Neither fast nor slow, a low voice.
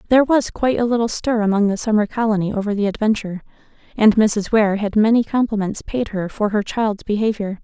No: average, 195 wpm; high, 215 Hz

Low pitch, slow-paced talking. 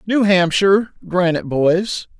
No: medium, 185 Hz; slow, 110 wpm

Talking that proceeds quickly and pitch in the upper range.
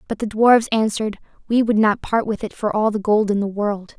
Yes: fast, 255 wpm; high, 215 Hz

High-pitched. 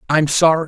No: medium, 155 Hz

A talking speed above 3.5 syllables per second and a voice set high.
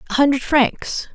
Yes: 4.4 syllables/s; very high, 275 Hz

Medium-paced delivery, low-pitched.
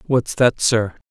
Yes: average, 165 wpm; low, 120 Hz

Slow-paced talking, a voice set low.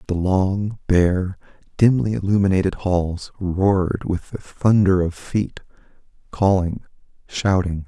Yes: slow, 105 wpm; very low, 95 Hz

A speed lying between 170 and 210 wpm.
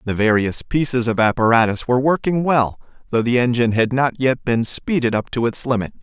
Yes: average, 200 wpm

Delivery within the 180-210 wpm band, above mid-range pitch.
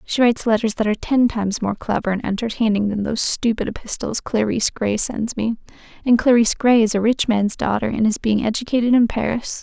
Yes: average, 200 wpm; high, 220 Hz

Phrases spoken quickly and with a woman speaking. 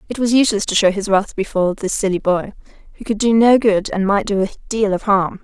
Yes: fast, 255 wpm; female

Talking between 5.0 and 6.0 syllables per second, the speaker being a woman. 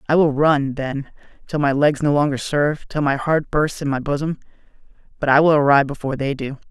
No: 5.9 syllables/s; male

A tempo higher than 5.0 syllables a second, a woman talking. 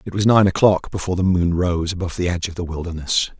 No: 6.8 syllables/s; male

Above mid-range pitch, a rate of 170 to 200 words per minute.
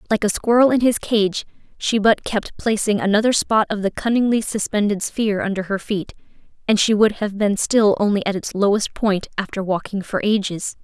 Yes: high, 210 Hz; average, 195 wpm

